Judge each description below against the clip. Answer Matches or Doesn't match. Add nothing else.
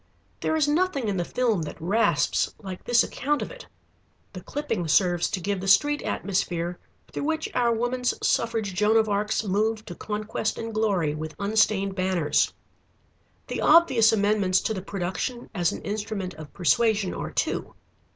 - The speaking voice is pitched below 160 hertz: Doesn't match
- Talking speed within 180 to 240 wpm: Doesn't match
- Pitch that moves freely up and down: Doesn't match